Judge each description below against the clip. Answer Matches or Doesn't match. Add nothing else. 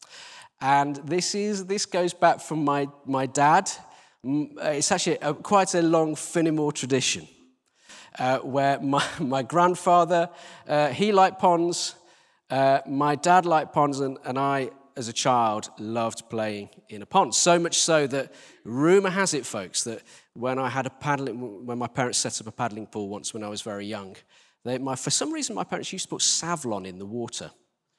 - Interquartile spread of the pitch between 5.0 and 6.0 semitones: Matches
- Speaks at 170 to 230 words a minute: Matches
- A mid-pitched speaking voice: Matches